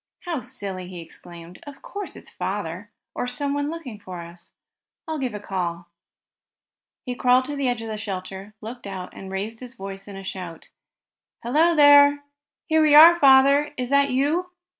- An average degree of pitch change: No, wide, 6.9 semitones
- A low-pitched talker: No, high, 245 Hz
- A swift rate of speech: No, average, 175 wpm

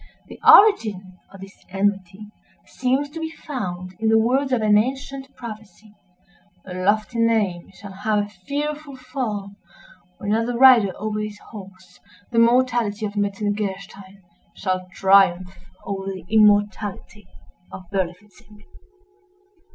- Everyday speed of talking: No, slow, 125 wpm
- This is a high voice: Yes, high, 210 Hz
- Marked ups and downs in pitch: No, average, 3.2 semitones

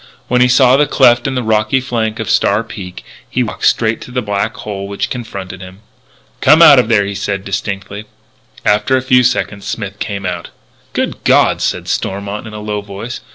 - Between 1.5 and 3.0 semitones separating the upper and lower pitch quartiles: No, average, 3.8 semitones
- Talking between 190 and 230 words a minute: Yes, average, 200 wpm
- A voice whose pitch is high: No, low, 105 Hz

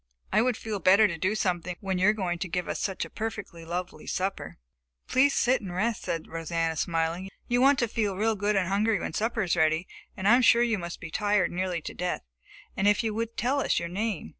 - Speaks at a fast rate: Yes, fast, 240 wpm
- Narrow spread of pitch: No, average, 4.0 semitones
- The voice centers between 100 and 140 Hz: No, high, 195 Hz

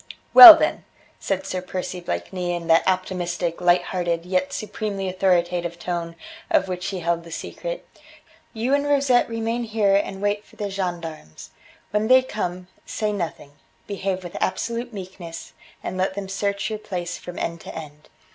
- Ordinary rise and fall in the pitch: Yes, average, 3.3 semitones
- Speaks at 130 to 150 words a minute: No, average, 165 wpm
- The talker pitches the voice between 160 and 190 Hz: Yes, medium, 185 Hz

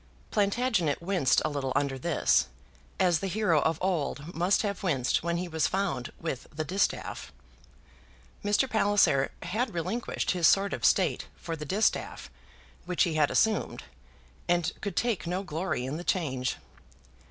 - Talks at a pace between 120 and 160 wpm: Yes, average, 155 wpm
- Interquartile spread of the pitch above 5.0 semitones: No, average, 4.5 semitones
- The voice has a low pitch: No, medium, 175 Hz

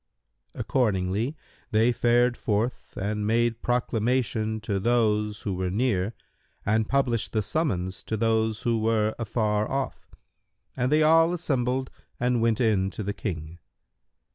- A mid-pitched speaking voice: No, low, 110 Hz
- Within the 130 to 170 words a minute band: Yes, slow, 135 wpm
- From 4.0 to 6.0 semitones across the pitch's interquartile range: No, average, 2.7 semitones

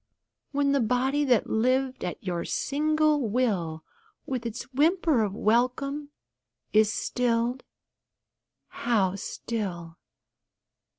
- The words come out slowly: Yes, slow, 100 wpm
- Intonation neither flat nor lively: Yes, average, 4.6 semitones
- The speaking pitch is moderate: No, high, 245 Hz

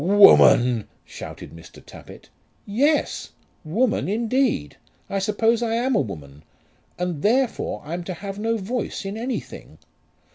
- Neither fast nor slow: No, slow, 130 wpm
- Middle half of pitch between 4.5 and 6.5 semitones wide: Yes, wide, 5.4 semitones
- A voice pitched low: No, high, 205 Hz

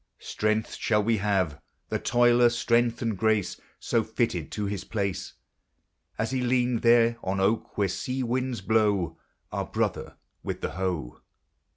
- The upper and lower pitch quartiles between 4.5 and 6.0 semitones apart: No, average, 3.4 semitones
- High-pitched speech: No, low, 110 Hz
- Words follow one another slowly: No, average, 150 wpm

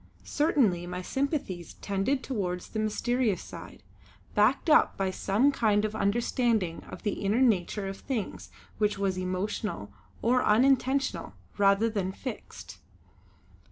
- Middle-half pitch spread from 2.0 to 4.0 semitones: No, average, 4.6 semitones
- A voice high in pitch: Yes, high, 210 Hz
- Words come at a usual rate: No, slow, 125 wpm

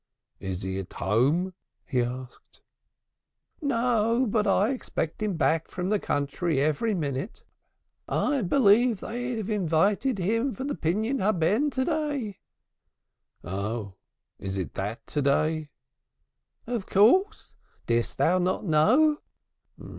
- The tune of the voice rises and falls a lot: Yes, wide, 8.8 semitones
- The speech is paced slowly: Yes, slow, 120 wpm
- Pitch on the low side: No, high, 190 Hz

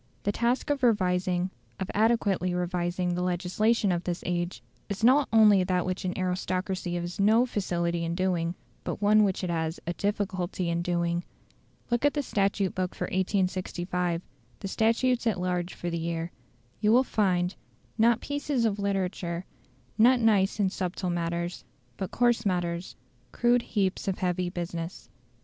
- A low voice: No, medium, 185 Hz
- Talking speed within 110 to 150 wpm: No, average, 160 wpm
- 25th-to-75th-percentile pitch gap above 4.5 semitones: No, average, 3.2 semitones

